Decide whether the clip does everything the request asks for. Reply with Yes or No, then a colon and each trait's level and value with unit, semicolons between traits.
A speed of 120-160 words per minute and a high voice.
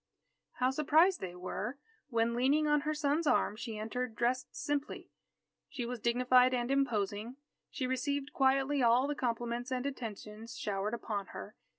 Yes: average, 155 wpm; very high, 250 Hz